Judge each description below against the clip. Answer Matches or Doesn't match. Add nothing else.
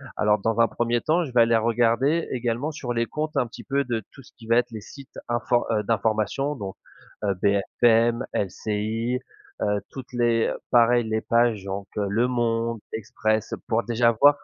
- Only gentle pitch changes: Matches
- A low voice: Matches